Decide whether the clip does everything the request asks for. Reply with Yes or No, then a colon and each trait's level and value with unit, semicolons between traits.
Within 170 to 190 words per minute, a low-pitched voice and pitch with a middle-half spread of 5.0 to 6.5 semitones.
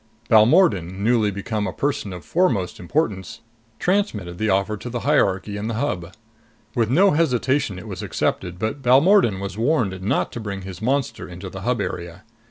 Yes: average, 175 wpm; low, 110 Hz; wide, 5.6 semitones